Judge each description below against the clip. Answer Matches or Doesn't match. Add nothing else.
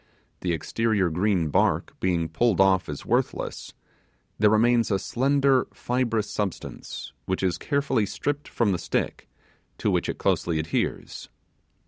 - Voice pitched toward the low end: Matches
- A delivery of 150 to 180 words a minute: Doesn't match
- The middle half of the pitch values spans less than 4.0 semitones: Doesn't match